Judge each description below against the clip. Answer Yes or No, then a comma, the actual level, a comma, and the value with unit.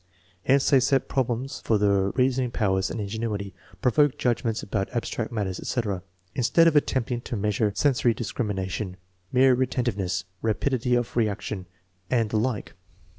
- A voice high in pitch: No, low, 115 Hz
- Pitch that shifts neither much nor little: Yes, average, 3.8 semitones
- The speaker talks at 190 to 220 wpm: No, average, 140 wpm